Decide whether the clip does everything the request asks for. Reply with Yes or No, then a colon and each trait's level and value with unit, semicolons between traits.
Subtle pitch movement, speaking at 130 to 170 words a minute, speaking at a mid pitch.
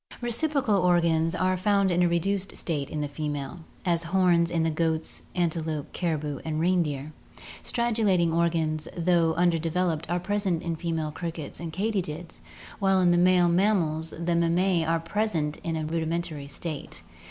Yes: narrow, 2.3 semitones; average, 150 wpm; medium, 170 Hz